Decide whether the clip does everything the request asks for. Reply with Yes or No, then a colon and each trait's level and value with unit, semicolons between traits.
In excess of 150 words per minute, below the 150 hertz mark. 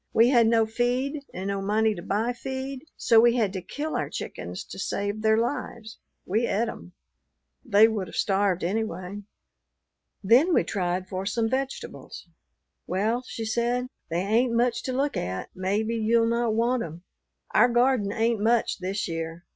No: average, 170 wpm; high, 225 Hz